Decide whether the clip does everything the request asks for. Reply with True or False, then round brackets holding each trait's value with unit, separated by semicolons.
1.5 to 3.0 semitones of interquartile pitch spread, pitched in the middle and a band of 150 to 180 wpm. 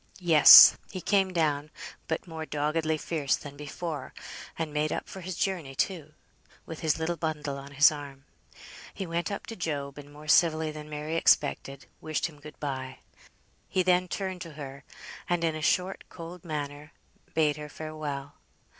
True (2.5 semitones; 155 Hz; 170 wpm)